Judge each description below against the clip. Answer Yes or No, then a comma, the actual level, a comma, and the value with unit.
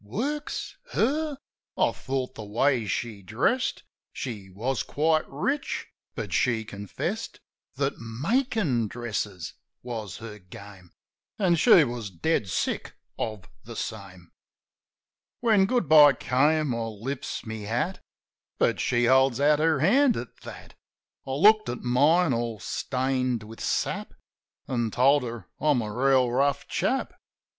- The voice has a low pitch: Yes, low, 130 Hz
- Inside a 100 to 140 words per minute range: Yes, slow, 135 wpm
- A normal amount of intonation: No, wide, 5.8 semitones